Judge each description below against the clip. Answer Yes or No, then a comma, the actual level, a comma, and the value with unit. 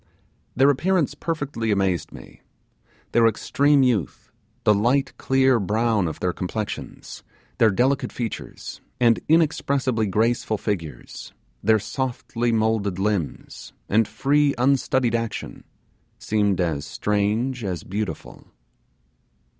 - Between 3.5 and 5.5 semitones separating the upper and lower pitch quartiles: Yes, average, 4.4 semitones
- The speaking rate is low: Yes, slow, 105 wpm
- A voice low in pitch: Yes, low, 115 Hz